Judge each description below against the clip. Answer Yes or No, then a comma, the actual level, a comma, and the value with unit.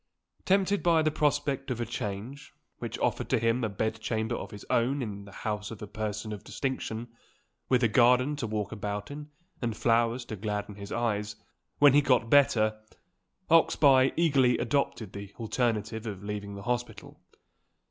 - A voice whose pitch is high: No, low, 115 Hz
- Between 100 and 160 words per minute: No, average, 170 wpm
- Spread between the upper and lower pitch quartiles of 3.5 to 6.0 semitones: Yes, average, 4.0 semitones